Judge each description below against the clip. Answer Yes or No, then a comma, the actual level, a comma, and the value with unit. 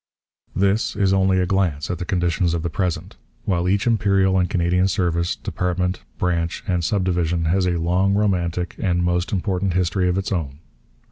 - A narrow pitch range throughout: Yes, narrow, 1.9 semitones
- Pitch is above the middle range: No, very low, 90 Hz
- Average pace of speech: Yes, average, 180 wpm